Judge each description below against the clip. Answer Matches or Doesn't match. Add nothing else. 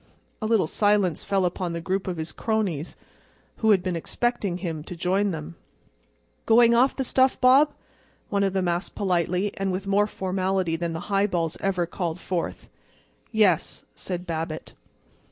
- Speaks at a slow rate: Doesn't match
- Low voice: Doesn't match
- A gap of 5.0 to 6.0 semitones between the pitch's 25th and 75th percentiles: Doesn't match